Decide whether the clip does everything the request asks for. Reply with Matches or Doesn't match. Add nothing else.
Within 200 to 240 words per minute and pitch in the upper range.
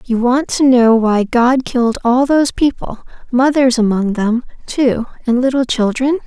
Doesn't match